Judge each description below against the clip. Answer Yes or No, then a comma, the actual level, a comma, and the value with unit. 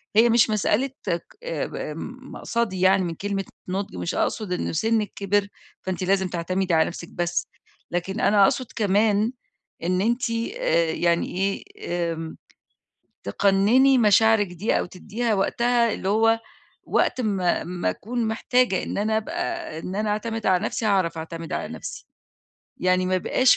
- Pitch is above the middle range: Yes, high, 200 Hz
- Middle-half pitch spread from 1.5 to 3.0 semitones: No, average, 3.8 semitones